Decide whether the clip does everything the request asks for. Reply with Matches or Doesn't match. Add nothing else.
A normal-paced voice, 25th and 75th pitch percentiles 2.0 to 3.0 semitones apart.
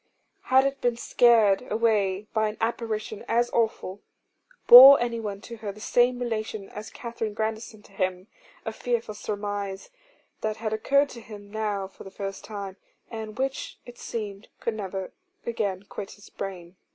Matches